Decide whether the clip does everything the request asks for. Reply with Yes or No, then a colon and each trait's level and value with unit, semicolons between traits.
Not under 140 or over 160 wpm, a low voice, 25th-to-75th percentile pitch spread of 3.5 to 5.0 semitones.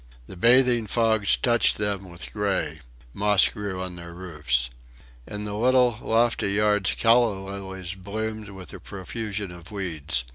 No: average, 145 wpm; low, 100 Hz; average, 3.1 semitones